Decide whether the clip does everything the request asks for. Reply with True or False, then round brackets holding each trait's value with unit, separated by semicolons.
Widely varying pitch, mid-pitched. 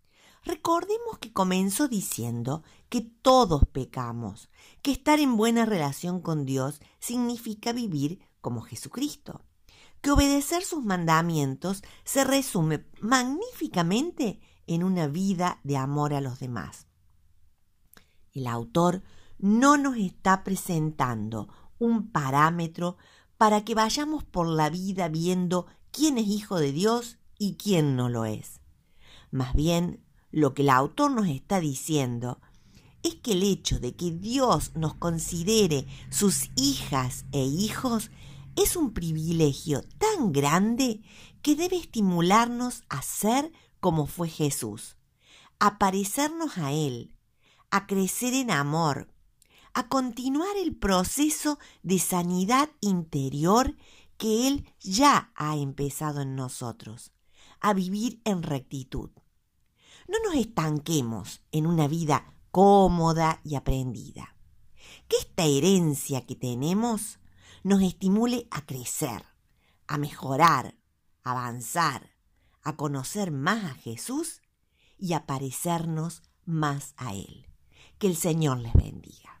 True (8.3 semitones; 170 Hz)